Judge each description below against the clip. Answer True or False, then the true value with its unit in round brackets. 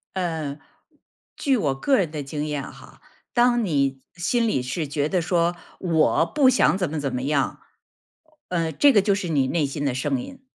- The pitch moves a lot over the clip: True (6.0 semitones)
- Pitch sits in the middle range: True (165 Hz)